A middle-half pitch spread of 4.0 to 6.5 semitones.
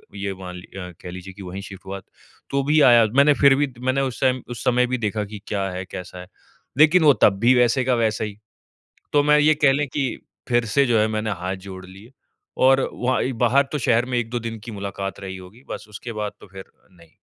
Yes: average, 5.2 semitones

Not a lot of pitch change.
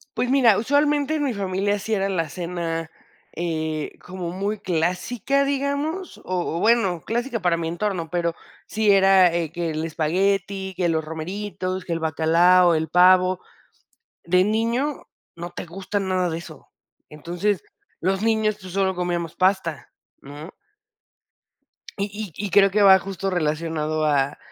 No: average, 3.6 semitones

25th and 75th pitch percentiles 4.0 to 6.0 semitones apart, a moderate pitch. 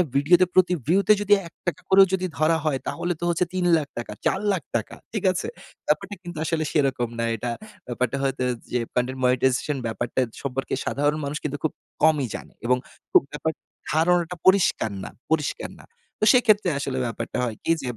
Yes: average, 5.3 semitones; medium, 155 Hz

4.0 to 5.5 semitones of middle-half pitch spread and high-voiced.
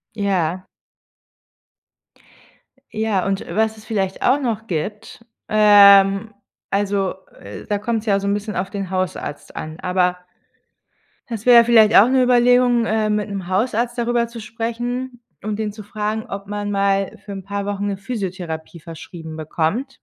No: average, 2.8 semitones; high, 205 Hz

